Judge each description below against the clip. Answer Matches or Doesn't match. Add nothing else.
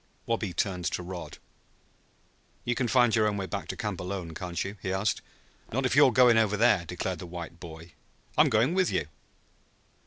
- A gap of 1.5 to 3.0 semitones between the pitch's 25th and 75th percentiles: Doesn't match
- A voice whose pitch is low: Matches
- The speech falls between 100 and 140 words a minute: Doesn't match